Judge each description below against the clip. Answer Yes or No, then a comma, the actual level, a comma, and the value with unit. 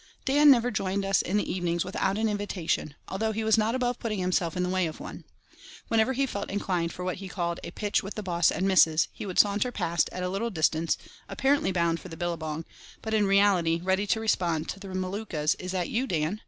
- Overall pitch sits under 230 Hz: Yes, high, 190 Hz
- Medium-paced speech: No, fast, 230 wpm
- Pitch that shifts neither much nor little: Yes, average, 3.7 semitones